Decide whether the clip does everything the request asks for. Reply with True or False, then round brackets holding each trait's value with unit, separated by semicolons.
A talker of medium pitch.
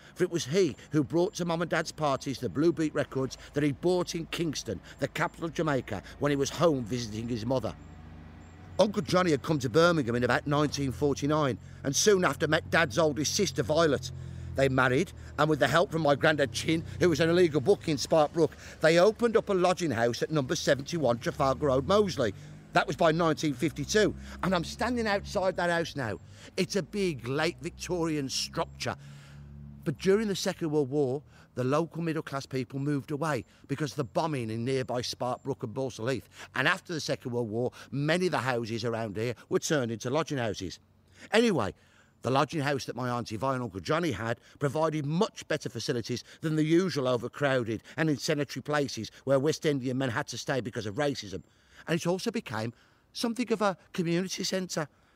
True (145 Hz)